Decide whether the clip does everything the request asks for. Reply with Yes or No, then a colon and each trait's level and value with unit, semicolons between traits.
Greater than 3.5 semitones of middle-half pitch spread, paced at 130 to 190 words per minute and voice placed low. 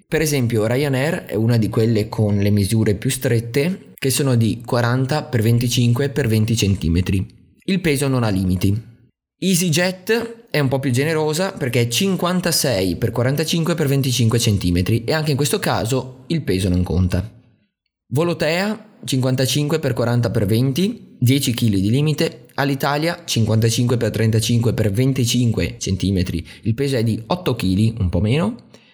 Yes: wide, 5.5 semitones; average, 155 wpm; low, 125 Hz